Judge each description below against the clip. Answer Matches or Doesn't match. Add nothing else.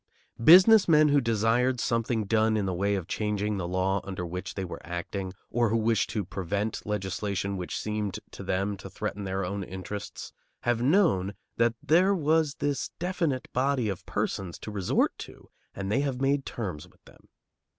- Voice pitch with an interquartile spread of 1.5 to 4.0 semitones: Doesn't match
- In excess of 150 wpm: Matches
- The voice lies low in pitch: Matches